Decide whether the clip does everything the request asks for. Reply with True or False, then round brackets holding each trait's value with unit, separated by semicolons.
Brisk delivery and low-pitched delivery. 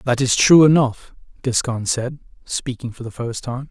False (180 wpm; 125 Hz)